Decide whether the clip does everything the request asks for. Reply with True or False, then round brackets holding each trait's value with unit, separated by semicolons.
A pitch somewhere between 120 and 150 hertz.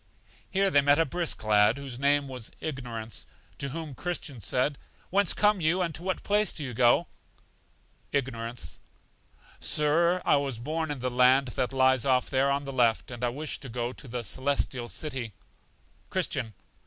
True (135 Hz)